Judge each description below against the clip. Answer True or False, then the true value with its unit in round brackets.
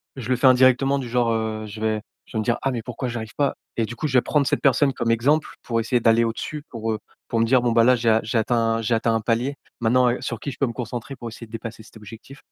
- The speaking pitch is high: False (115 Hz)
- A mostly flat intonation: True (2.2 semitones)